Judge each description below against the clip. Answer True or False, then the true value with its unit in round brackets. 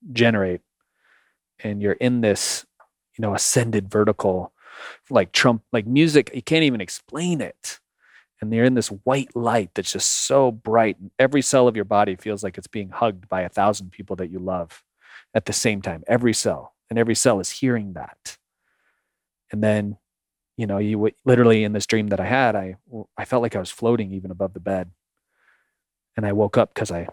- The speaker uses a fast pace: False (190 wpm)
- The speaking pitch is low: True (110 Hz)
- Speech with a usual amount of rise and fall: True (3.5 semitones)